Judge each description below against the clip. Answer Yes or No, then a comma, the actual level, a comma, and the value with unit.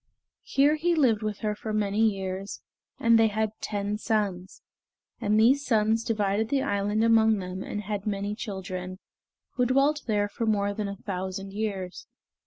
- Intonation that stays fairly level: Yes, narrow, 2.0 semitones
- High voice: Yes, high, 210 Hz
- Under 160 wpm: No, average, 165 wpm